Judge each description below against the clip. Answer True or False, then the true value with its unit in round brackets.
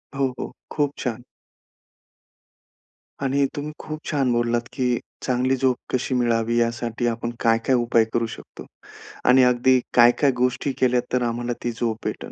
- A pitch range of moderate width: False (1.7 semitones)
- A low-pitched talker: True (125 Hz)